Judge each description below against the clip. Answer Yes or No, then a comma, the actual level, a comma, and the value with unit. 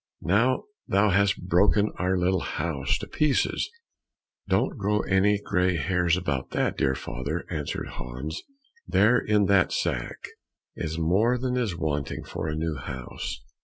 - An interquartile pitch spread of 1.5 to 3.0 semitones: No, average, 5.0 semitones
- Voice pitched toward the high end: No, very low, 90 Hz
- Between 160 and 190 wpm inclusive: No, average, 145 wpm